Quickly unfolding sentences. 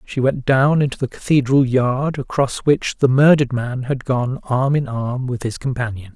No: average, 195 wpm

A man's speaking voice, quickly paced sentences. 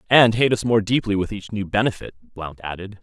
Yes: male; fast, 220 wpm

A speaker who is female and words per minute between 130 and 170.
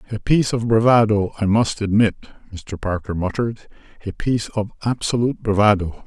No: male; average, 140 wpm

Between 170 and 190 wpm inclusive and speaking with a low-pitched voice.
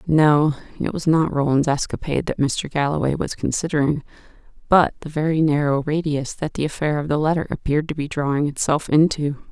No: average, 175 wpm; medium, 150 Hz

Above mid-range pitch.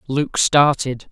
No: low, 135 Hz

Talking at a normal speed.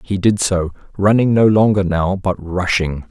Yes: average, 175 wpm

